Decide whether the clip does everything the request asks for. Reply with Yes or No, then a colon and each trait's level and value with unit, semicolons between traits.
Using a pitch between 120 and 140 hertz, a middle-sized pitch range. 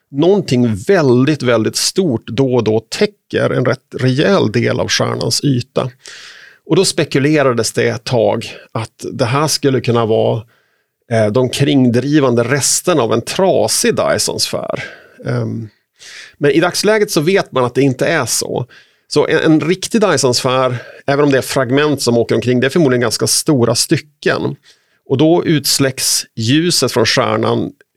Yes: low, 135 Hz; average, 4.6 semitones